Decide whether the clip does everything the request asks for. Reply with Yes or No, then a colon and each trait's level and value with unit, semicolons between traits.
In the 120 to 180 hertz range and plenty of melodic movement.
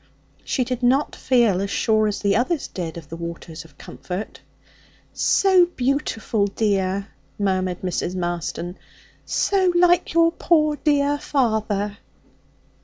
No: high, 215 Hz; wide, 7.5 semitones